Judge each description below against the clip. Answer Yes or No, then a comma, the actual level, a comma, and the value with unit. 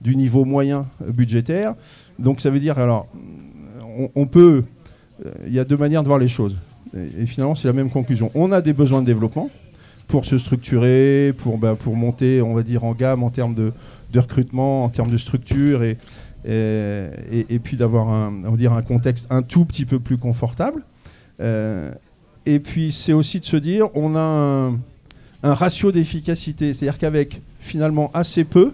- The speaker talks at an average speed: Yes, average, 200 wpm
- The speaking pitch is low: Yes, low, 130 Hz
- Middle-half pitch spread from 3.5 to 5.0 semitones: Yes, average, 3.9 semitones